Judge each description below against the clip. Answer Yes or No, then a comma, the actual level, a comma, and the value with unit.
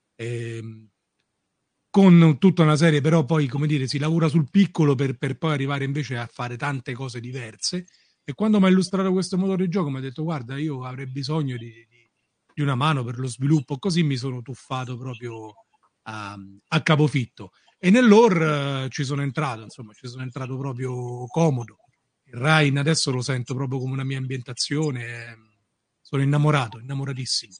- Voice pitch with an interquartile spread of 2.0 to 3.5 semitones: No, average, 3.9 semitones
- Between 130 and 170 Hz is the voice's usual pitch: Yes, low, 135 Hz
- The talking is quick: Yes, fast, 175 wpm